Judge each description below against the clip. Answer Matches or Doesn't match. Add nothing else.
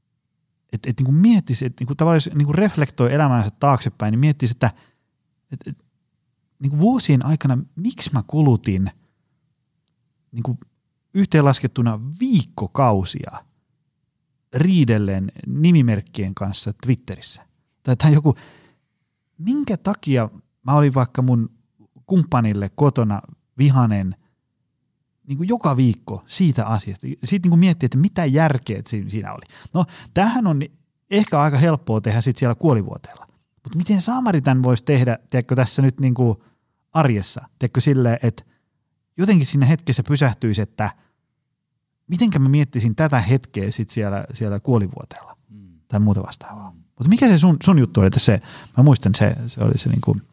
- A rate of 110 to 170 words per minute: Matches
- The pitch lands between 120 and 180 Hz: Matches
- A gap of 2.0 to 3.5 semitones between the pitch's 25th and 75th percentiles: Doesn't match